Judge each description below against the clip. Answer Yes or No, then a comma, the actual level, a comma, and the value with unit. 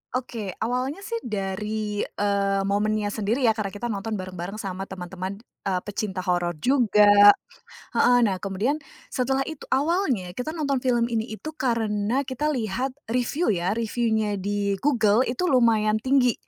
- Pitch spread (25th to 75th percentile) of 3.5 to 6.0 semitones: Yes, average, 4.0 semitones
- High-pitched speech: Yes, high, 215 Hz